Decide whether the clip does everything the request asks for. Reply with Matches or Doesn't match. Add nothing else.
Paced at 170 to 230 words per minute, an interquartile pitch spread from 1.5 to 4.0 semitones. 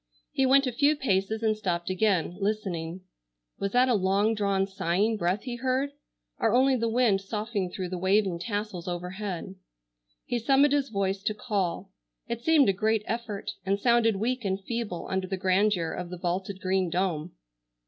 Matches